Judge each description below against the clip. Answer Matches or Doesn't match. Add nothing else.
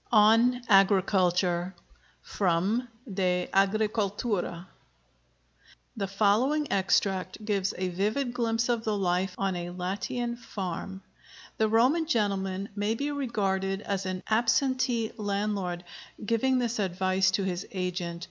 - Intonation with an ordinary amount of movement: Matches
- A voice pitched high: Matches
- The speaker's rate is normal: Doesn't match